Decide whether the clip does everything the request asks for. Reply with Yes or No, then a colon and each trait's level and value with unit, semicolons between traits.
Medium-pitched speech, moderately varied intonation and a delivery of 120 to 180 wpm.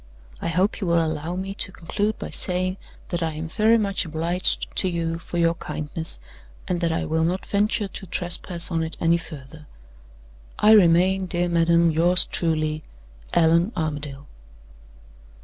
No: medium, 170 Hz; narrow, 2.3 semitones; average, 160 wpm